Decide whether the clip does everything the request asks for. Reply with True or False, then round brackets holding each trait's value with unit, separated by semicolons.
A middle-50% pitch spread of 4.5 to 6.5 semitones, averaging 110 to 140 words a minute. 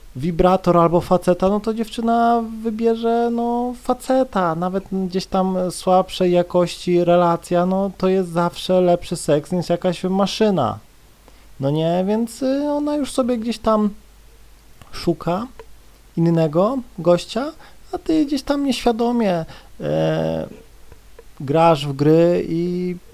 True (5.0 semitones; 115 wpm)